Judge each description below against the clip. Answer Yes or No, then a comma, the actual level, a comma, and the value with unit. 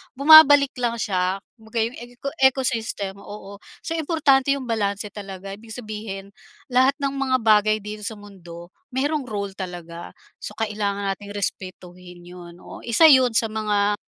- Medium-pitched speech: No, high, 215 Hz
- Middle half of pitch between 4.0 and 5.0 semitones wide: Yes, average, 4.5 semitones